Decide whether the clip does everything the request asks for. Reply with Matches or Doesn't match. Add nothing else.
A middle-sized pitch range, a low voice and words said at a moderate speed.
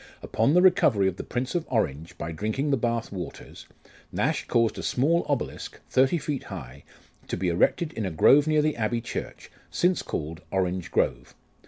Doesn't match